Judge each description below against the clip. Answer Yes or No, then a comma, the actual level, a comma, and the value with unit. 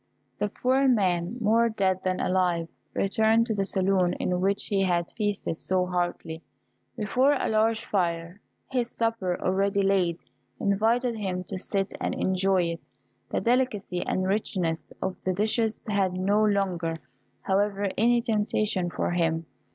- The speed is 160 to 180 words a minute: No, average, 145 wpm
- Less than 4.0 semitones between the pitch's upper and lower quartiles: Yes, average, 3.1 semitones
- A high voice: Yes, high, 195 Hz